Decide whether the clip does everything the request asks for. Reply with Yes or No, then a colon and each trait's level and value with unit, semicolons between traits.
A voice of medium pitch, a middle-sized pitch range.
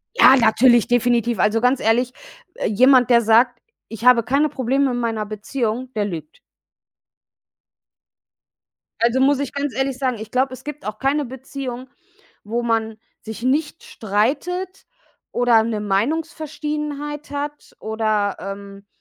No: high, 245 Hz; average, 3.9 semitones